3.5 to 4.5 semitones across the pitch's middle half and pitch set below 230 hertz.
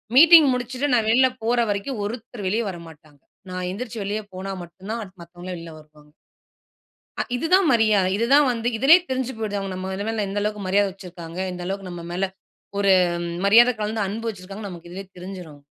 Yes: average, 4.0 semitones; high, 200 Hz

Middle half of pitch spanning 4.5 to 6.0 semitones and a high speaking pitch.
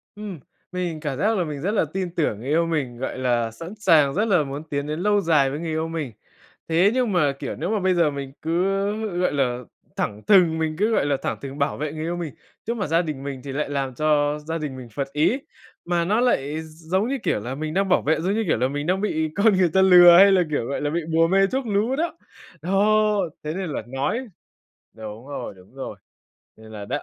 No: average, 5.1 semitones; medium, 160 Hz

